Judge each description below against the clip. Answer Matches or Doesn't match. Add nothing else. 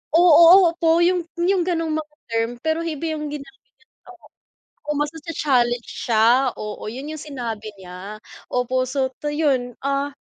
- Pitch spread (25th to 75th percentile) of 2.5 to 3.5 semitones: Doesn't match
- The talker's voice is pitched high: Matches